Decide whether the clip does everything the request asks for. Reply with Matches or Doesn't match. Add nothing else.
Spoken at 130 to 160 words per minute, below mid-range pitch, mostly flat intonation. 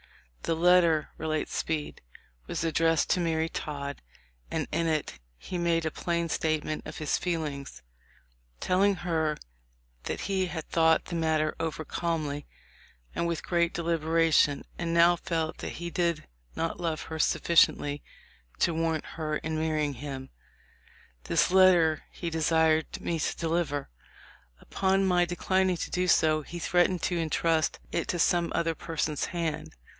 Doesn't match